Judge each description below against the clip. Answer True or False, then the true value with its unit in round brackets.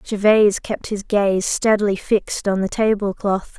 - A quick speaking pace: False (165 wpm)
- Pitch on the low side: False (205 Hz)